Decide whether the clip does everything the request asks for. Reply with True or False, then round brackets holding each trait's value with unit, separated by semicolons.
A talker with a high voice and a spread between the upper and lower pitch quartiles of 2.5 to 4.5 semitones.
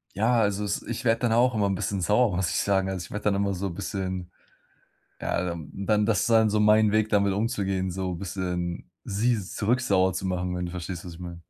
False (100 Hz; 2.8 semitones)